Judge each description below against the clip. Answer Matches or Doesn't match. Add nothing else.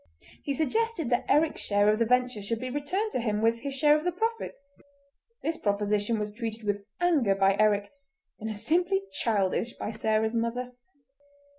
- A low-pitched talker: Doesn't match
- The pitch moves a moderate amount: Doesn't match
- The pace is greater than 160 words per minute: Matches